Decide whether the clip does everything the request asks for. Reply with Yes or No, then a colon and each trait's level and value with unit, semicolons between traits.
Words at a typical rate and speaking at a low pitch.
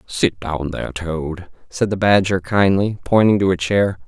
Yes: average, 175 wpm; very low, 90 Hz